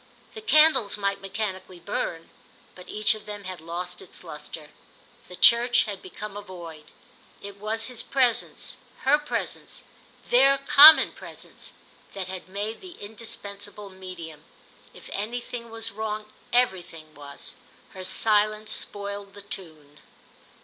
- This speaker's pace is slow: Yes, slow, 130 wpm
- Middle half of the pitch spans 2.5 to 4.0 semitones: Yes, average, 3.5 semitones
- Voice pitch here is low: No, high, 205 Hz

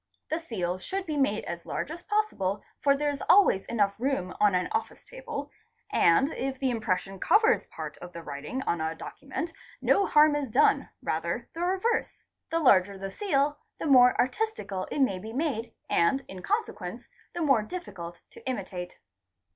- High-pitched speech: Yes, very high, 265 Hz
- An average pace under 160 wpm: No, average, 175 wpm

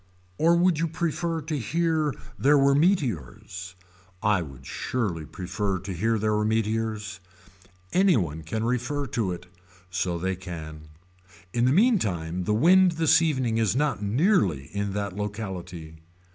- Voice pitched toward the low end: Yes, low, 110 Hz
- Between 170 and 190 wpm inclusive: No, average, 145 wpm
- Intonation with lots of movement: Yes, wide, 8.5 semitones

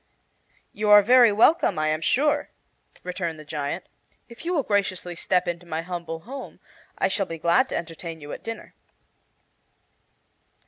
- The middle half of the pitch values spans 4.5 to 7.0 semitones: Yes, average, 4.9 semitones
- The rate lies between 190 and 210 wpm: No, average, 155 wpm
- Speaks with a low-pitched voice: No, medium, 180 Hz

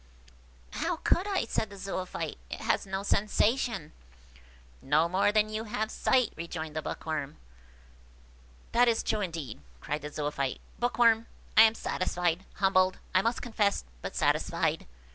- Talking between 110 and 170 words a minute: Yes, average, 140 wpm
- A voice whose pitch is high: Yes, high, 195 Hz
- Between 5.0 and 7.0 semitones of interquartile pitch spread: Yes, wide, 5.5 semitones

